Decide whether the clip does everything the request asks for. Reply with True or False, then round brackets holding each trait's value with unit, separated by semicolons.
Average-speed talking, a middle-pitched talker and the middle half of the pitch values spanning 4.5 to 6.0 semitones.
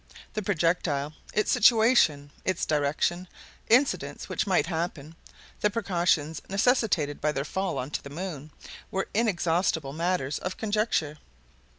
False (125 wpm; 175 Hz; 5.1 semitones)